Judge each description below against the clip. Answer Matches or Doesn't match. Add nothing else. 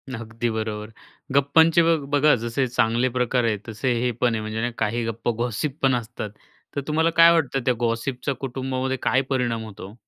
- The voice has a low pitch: Matches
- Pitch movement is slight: Doesn't match